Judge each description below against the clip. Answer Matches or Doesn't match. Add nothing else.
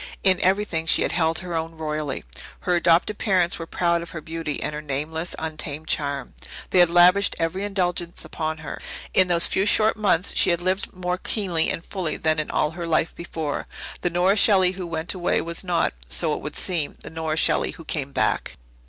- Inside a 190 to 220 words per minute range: Matches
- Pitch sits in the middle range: Matches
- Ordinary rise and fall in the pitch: Doesn't match